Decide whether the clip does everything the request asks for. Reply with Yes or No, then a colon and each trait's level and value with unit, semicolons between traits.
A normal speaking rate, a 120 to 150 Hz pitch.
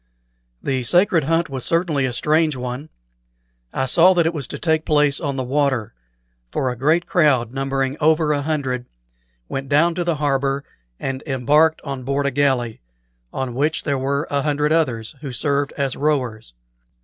Yes: average, 175 wpm; medium, 140 Hz